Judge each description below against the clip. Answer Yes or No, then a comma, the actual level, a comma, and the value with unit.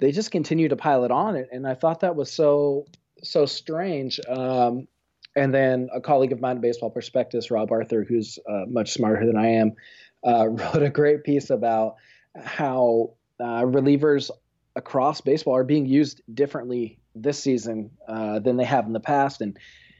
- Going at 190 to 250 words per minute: No, average, 175 wpm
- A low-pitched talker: Yes, low, 130 Hz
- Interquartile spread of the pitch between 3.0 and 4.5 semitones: Yes, average, 3.8 semitones